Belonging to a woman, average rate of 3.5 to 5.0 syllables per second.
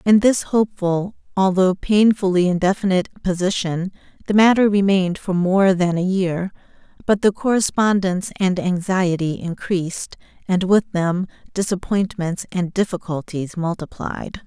Yes: female; 4.7 syllables/s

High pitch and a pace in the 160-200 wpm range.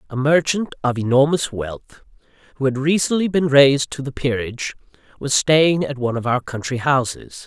No: low, 135 Hz; average, 170 wpm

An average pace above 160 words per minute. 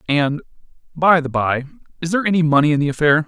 Yes: average, 200 wpm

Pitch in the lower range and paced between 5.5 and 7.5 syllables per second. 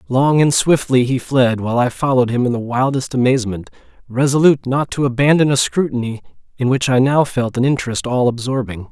Yes: low, 130 Hz; 5.9 syllables/s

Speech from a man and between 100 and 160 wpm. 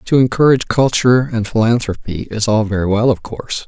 No: male; average, 180 wpm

